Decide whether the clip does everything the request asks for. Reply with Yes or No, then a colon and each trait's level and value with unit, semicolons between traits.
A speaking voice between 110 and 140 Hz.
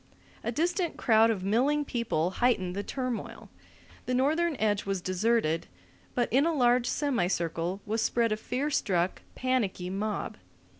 No: high, 230 Hz